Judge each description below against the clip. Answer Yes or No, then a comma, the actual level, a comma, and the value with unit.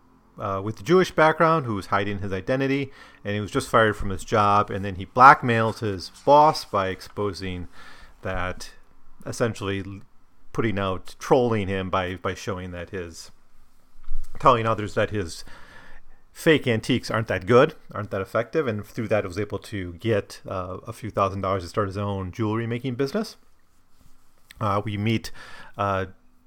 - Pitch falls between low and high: No, low, 100 Hz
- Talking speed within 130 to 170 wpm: Yes, average, 165 wpm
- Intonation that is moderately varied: Yes, average, 3.3 semitones